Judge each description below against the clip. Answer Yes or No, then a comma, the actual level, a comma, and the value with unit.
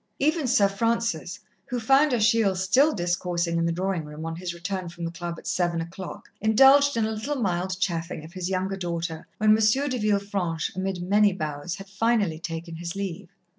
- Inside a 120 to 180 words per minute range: No, average, 190 wpm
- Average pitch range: Yes, average, 4.2 semitones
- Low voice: No, high, 190 Hz